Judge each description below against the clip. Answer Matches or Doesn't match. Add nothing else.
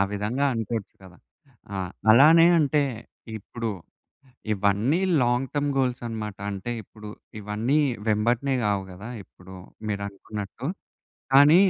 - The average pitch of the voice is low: Matches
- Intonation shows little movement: Doesn't match